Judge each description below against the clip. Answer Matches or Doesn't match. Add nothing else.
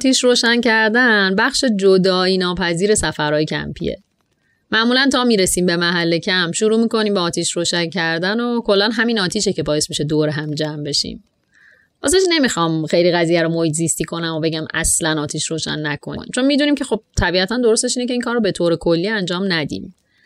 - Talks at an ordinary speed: Doesn't match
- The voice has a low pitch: Doesn't match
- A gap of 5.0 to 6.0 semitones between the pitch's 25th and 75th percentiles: Matches